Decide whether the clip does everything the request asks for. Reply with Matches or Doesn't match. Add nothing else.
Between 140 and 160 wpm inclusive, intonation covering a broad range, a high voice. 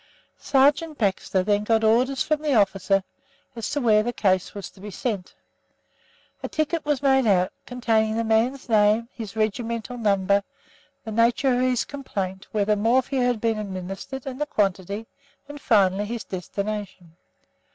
Doesn't match